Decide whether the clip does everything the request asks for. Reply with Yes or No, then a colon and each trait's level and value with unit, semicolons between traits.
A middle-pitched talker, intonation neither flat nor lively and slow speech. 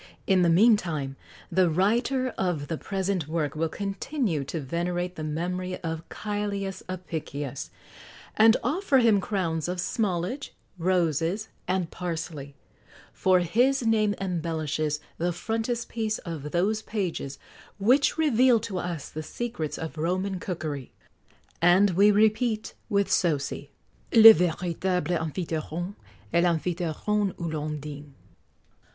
Yes: medium, 180 Hz; average, 4.3 semitones; slow, 120 wpm